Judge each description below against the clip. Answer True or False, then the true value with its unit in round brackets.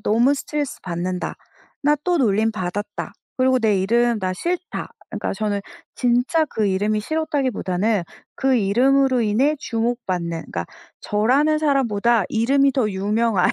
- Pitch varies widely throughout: False (4.9 semitones)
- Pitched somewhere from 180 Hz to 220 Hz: False (230 Hz)